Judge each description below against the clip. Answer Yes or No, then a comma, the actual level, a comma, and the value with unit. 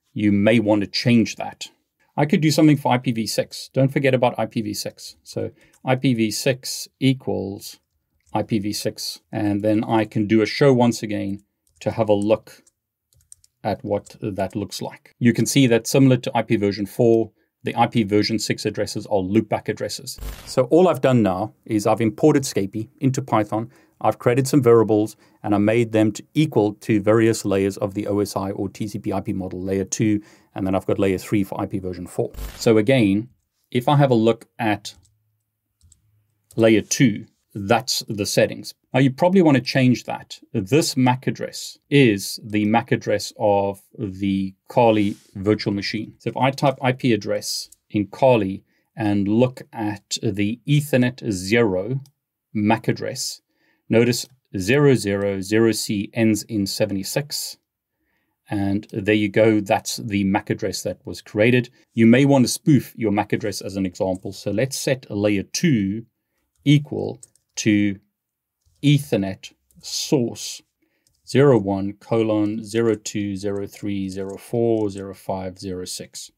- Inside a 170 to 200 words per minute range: No, average, 145 wpm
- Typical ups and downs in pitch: Yes, average, 3.3 semitones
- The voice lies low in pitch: Yes, low, 110 Hz